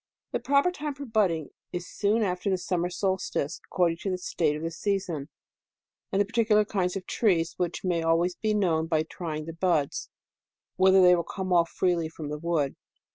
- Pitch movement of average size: Yes, average, 3.1 semitones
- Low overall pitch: No, medium, 180 Hz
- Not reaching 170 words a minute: No, average, 190 wpm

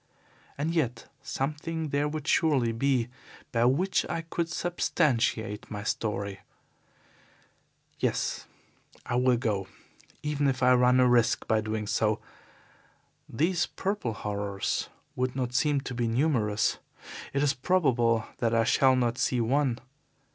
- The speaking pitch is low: Yes, low, 125 Hz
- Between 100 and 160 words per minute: Yes, slow, 135 wpm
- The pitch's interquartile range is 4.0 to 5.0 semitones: Yes, average, 4.4 semitones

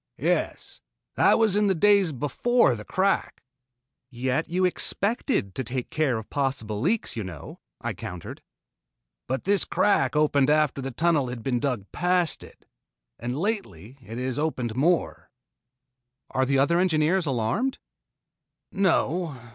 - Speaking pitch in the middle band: Yes, medium, 145 Hz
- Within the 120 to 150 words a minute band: Yes, average, 140 wpm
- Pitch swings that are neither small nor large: No, wide, 6.5 semitones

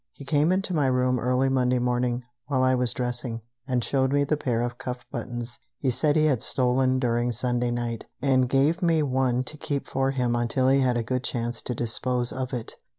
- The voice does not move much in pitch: Yes, narrow, 1.8 semitones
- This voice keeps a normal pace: No, fast, 215 wpm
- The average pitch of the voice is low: Yes, low, 125 Hz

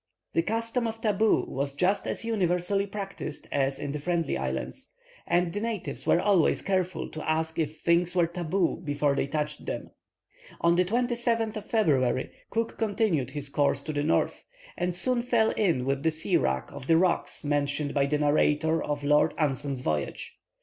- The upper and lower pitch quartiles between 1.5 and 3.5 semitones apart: No, wide, 5.6 semitones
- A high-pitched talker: No, medium, 165 Hz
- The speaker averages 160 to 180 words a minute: Yes, average, 175 wpm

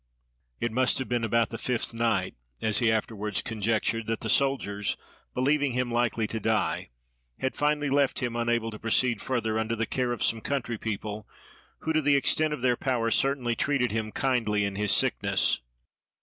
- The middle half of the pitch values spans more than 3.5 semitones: No, average, 2.8 semitones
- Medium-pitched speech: No, low, 115 Hz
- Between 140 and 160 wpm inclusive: No, average, 180 wpm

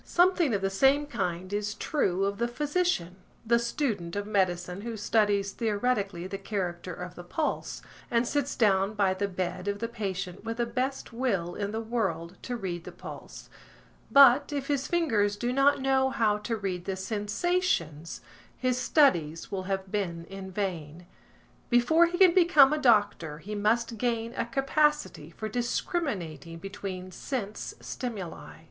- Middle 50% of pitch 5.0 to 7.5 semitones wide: Yes, average, 5.3 semitones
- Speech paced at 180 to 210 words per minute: No, average, 160 wpm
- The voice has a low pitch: No, high, 210 Hz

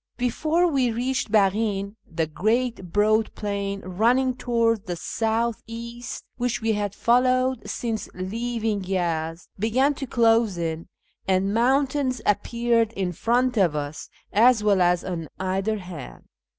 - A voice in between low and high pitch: No, high, 220 Hz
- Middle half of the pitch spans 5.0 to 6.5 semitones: No, average, 4.2 semitones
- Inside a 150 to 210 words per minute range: No, slow, 135 wpm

